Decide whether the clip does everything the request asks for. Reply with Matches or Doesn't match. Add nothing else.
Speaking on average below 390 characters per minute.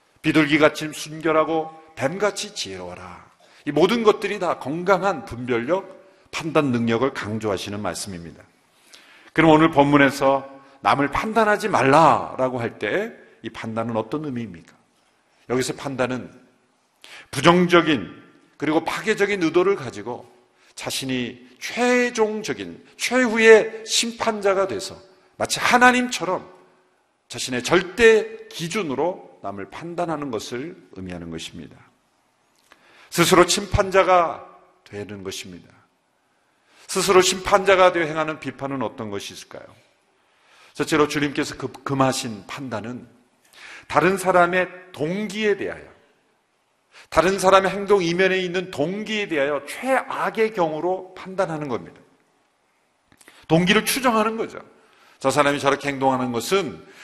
Matches